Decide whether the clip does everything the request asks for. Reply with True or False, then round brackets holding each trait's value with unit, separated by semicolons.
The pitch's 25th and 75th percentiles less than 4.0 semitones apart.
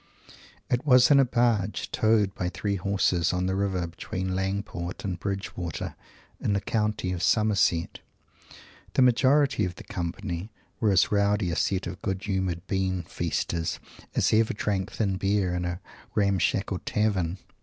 True (2.8 semitones)